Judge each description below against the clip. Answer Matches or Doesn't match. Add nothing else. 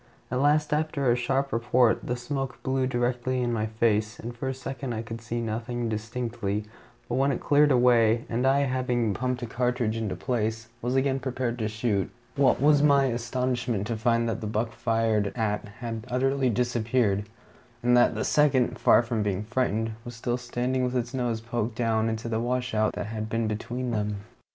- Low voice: Matches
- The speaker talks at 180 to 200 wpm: Matches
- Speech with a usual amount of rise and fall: Doesn't match